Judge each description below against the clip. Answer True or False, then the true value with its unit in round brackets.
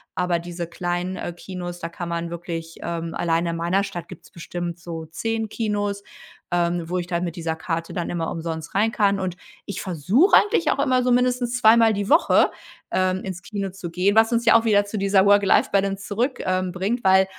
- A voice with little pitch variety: False (3.2 semitones)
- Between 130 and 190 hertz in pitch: True (185 Hz)